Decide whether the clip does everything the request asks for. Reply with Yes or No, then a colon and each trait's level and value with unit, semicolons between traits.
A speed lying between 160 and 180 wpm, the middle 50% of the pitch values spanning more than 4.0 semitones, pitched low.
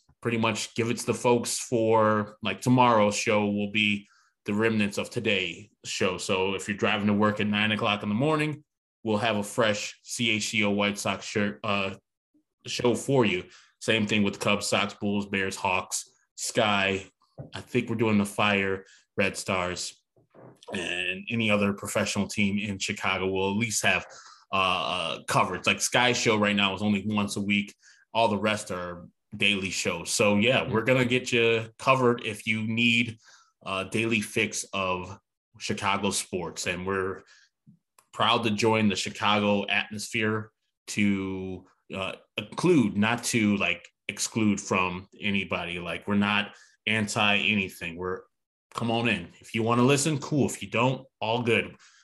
No: average, 165 wpm; narrow, 2.4 semitones; low, 105 Hz